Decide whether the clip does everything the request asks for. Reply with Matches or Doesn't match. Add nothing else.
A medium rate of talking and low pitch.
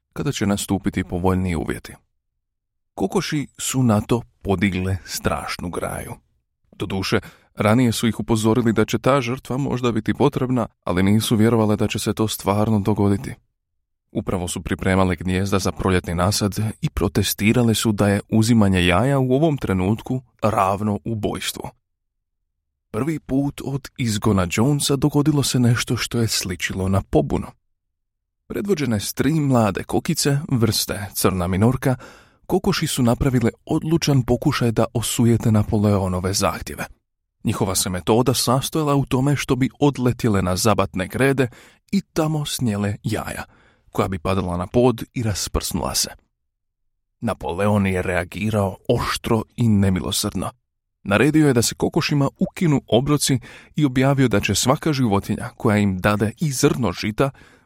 Matches